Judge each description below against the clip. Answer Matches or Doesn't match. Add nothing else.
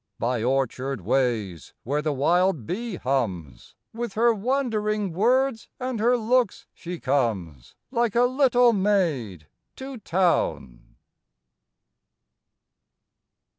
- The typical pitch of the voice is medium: Matches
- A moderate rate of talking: Doesn't match